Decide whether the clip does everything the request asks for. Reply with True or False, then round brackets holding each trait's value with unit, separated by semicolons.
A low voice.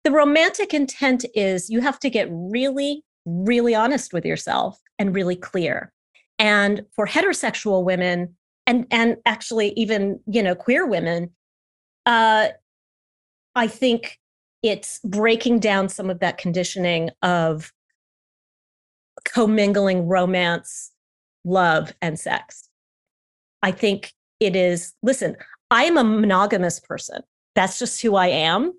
False (210 Hz)